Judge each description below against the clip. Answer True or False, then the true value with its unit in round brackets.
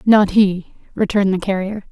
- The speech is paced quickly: False (155 wpm)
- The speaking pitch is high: True (195 Hz)